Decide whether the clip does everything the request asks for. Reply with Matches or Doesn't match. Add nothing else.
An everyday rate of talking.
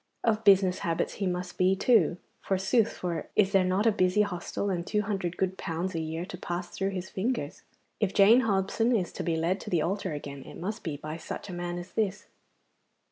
Doesn't match